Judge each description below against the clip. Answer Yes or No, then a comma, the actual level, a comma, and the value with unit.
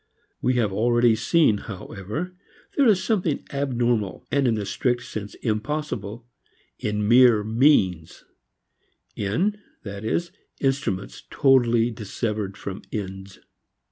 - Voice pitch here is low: Yes, low, 115 Hz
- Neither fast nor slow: No, slow, 110 wpm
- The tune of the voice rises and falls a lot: No, average, 4.6 semitones